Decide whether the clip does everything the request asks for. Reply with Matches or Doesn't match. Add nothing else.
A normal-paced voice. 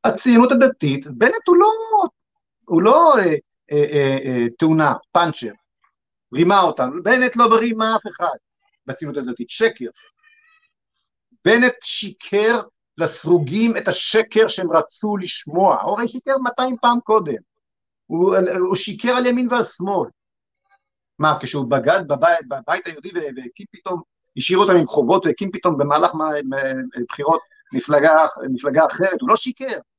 Matches